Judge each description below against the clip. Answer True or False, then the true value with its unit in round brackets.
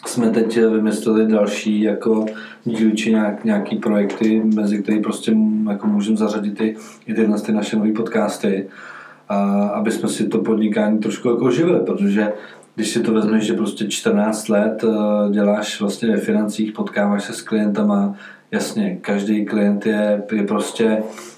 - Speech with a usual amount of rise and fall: False (1.3 semitones)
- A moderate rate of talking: True (155 wpm)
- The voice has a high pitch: False (110 Hz)